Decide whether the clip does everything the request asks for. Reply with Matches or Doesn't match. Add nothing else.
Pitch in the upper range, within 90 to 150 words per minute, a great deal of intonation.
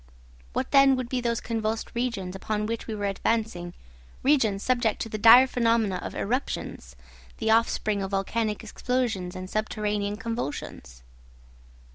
Doesn't match